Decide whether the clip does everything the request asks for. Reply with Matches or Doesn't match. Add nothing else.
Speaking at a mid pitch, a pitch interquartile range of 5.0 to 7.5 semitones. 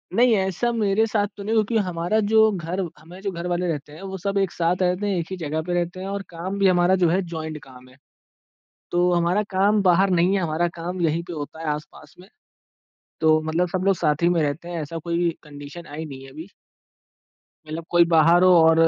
Doesn't match